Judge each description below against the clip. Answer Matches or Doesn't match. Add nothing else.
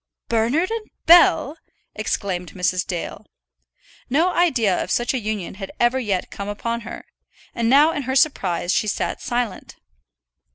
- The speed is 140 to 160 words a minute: Matches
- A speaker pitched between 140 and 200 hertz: Doesn't match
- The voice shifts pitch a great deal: Matches